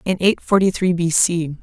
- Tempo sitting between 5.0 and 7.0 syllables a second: No, 4.7 syllables/s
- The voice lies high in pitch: No, medium, 175 Hz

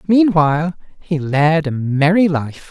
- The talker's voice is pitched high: No, medium, 160 Hz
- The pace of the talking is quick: No, slow, 135 wpm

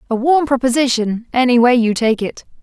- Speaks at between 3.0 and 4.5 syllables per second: No, 5.3 syllables/s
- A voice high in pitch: Yes, high, 245 Hz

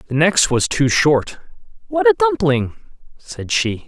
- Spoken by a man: Yes, male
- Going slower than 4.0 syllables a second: Yes, 3.7 syllables/s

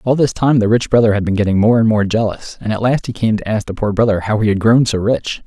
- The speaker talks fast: Yes, fast, 320 wpm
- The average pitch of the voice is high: No, low, 110 Hz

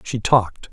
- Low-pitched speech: Yes, low, 110 Hz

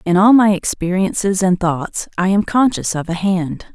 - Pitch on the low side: No, high, 190 Hz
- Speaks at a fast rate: No, average, 190 wpm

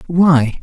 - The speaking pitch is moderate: Yes, medium, 155 Hz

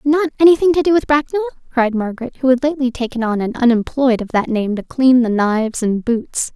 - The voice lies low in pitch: No, very high, 255 Hz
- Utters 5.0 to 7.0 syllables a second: Yes, 5.9 syllables/s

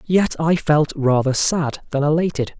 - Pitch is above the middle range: No, medium, 155 Hz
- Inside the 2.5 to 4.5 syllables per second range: Yes, 4.4 syllables/s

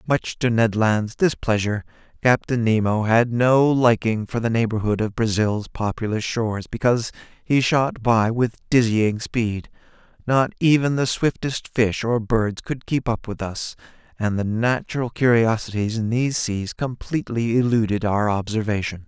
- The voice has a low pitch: Yes, low, 115 Hz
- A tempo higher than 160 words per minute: No, average, 150 wpm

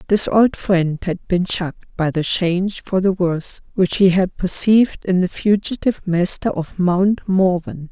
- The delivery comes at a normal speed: Yes, average, 175 wpm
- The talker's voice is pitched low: No, medium, 185 Hz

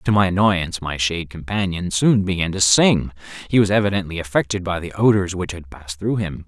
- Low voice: Yes, very low, 95 Hz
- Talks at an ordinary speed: Yes, average, 195 wpm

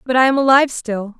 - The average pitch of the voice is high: Yes, very high, 250 Hz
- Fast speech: Yes, fast, 250 wpm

